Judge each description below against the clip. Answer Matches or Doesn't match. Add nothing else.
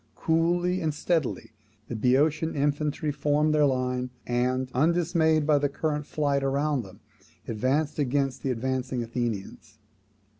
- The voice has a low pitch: Doesn't match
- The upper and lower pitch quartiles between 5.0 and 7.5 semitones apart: Doesn't match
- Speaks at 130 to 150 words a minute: Matches